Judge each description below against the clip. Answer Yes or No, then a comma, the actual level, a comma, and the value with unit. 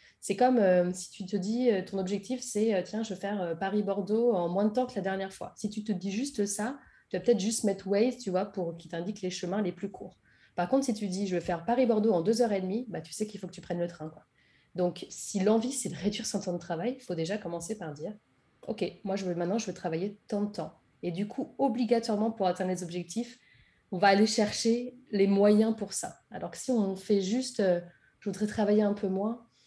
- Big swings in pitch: No, average, 3.3 semitones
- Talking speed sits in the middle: No, fast, 260 wpm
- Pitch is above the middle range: Yes, high, 200 Hz